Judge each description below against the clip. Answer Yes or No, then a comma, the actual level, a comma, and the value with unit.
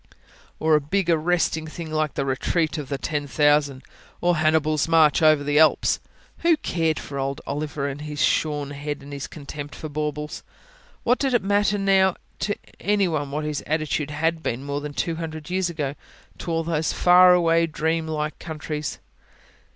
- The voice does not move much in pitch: Yes, narrow, 2.2 semitones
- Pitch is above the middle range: No, medium, 155 Hz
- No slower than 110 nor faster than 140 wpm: No, average, 175 wpm